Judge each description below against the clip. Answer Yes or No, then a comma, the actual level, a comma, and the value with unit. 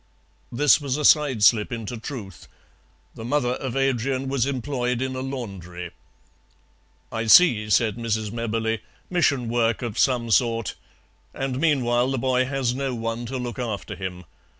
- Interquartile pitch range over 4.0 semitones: No, average, 2.8 semitones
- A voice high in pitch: No, low, 120 Hz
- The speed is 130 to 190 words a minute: Yes, average, 150 wpm